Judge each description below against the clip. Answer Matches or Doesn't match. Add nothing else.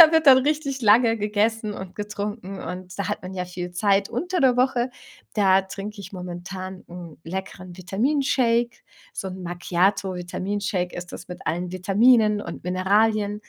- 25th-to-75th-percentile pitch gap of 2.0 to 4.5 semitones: Matches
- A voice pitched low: Doesn't match